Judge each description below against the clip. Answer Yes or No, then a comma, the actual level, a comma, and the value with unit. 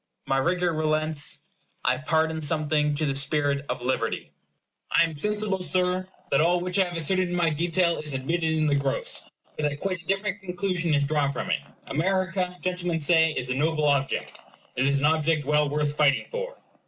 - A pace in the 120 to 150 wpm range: No, average, 190 wpm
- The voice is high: No, medium, 160 Hz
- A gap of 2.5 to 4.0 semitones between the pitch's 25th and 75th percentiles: Yes, average, 3.6 semitones